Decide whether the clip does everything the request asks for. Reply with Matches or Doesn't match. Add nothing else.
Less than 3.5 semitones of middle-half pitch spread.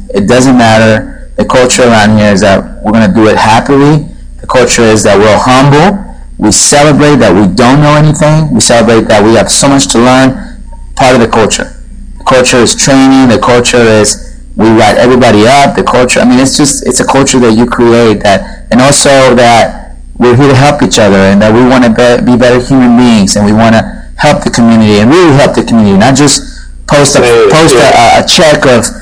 Doesn't match